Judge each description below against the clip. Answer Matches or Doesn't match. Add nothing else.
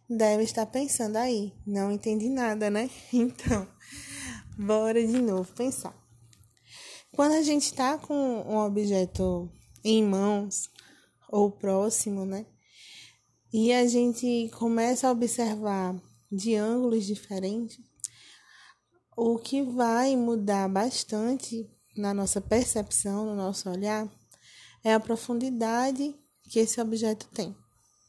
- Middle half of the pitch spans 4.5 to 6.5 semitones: Doesn't match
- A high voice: Matches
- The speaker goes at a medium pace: Doesn't match